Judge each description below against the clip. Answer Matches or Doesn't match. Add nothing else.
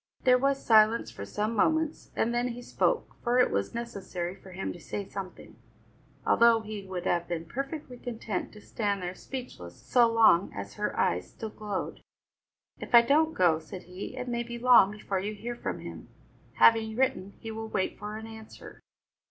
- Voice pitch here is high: Matches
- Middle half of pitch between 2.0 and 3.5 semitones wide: Doesn't match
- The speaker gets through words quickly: Doesn't match